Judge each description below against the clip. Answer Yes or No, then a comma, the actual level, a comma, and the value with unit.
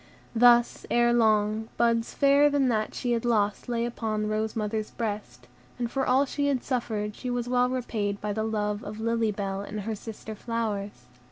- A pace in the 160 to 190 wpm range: Yes, average, 185 wpm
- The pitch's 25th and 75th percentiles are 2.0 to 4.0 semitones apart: Yes, narrow, 2.4 semitones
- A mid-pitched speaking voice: No, high, 225 Hz